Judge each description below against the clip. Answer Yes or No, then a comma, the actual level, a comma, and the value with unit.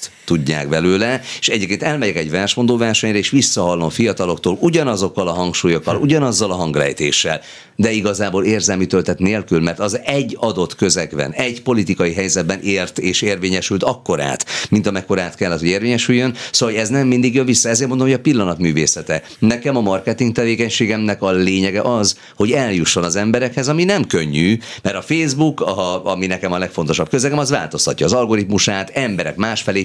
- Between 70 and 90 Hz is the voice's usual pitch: No, low, 105 Hz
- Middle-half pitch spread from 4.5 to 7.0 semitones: Yes, average, 4.9 semitones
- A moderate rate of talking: No, fast, 165 wpm